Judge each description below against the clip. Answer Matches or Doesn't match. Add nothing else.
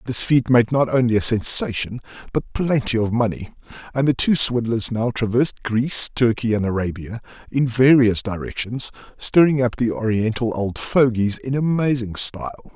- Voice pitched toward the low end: Matches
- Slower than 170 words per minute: Matches